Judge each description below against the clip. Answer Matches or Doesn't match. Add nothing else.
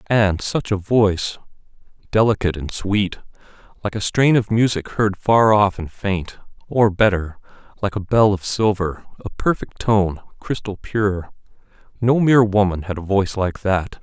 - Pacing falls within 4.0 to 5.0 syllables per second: Matches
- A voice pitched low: Matches